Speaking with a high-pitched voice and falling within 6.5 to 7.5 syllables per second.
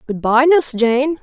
No: very high, 260 Hz; 4.6 syllables/s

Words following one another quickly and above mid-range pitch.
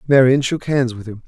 No: fast, 235 wpm; low, 125 Hz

